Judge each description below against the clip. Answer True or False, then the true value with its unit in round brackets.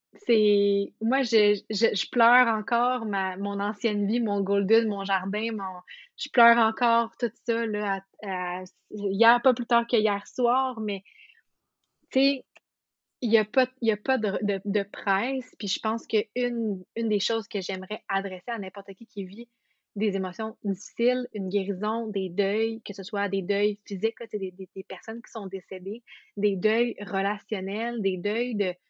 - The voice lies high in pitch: True (210 Hz)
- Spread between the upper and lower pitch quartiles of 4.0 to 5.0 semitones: False (2.7 semitones)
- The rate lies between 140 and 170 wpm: False (180 wpm)